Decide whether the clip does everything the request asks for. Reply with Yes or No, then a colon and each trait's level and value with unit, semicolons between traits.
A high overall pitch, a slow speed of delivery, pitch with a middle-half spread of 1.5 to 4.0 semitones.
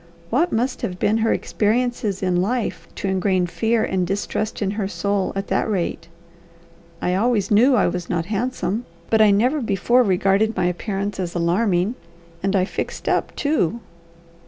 No: high, 200 Hz; average, 165 wpm; average, 3.5 semitones